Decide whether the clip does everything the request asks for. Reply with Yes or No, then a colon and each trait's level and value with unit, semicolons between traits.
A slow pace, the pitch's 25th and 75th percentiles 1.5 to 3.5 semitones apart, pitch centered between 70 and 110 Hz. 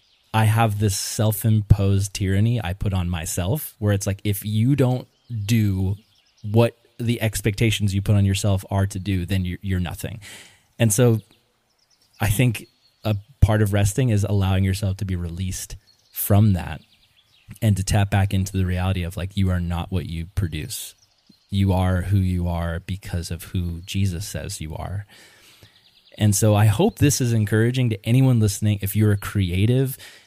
No: average, 175 wpm; narrow, 2.5 semitones; low, 100 Hz